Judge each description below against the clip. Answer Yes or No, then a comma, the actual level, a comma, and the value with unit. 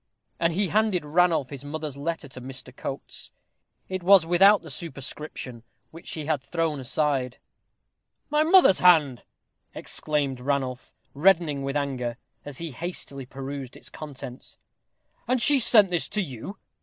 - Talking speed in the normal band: Yes, average, 145 wpm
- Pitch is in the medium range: Yes, medium, 150 Hz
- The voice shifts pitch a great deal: No, average, 4.6 semitones